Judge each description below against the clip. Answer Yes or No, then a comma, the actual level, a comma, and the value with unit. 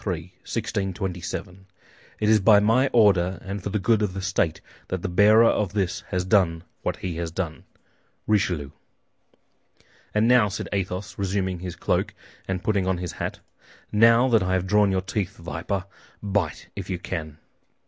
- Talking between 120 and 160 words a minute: No, average, 170 wpm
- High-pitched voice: No, very low, 95 Hz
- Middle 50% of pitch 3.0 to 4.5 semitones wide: No, narrow, 2.6 semitones